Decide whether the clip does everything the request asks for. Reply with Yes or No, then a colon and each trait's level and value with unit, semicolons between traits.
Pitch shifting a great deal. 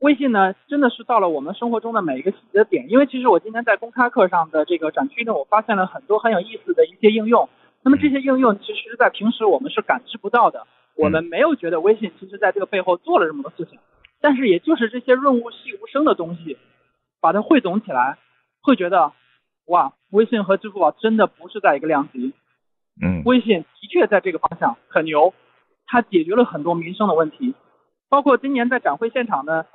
Yes: wide, 5.8 semitones